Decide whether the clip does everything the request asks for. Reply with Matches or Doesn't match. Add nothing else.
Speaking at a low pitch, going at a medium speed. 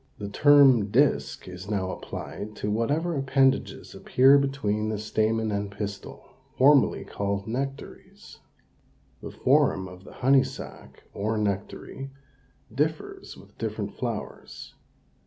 Doesn't match